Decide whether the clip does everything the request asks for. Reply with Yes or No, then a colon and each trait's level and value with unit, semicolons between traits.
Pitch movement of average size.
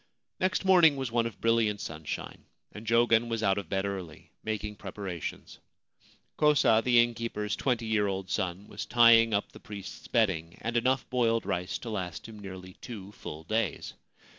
Yes: average, 3.3 semitones